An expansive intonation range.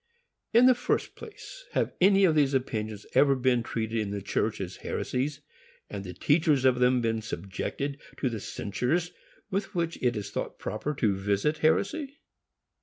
Yes: wide, 7.0 semitones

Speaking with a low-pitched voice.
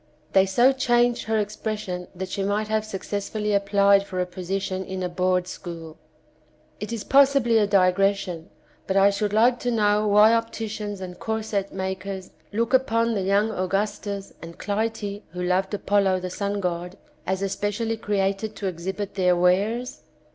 No: high, 200 Hz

